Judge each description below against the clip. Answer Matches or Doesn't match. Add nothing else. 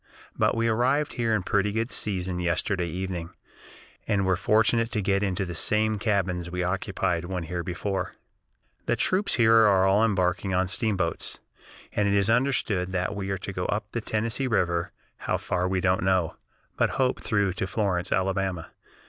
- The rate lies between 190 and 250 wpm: Doesn't match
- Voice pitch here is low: Matches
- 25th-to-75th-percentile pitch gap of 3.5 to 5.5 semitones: Doesn't match